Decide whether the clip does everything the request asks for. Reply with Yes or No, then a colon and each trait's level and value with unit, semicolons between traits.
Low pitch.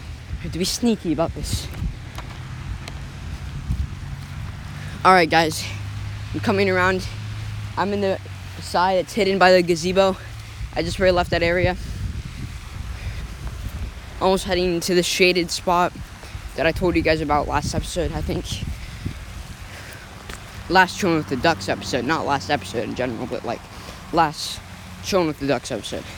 No: medium, 145 Hz